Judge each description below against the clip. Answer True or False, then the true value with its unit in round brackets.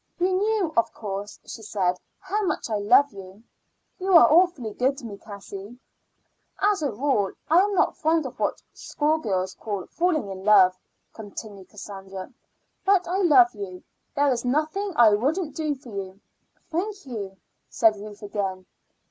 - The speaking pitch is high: True (235 Hz)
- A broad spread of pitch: True (8.2 semitones)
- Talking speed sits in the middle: True (160 wpm)